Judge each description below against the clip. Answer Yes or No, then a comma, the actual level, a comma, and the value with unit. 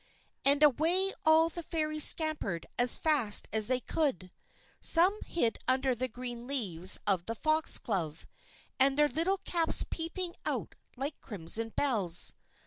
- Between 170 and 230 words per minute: No, slow, 135 wpm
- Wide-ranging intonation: Yes, wide, 6.2 semitones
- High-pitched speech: Yes, very high, 270 Hz